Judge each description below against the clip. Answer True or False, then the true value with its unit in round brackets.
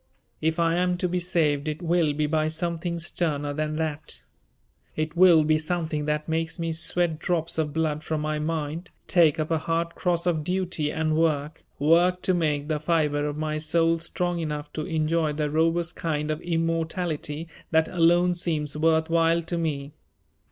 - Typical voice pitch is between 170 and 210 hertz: False (160 Hz)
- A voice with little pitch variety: True (1.7 semitones)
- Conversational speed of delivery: True (180 wpm)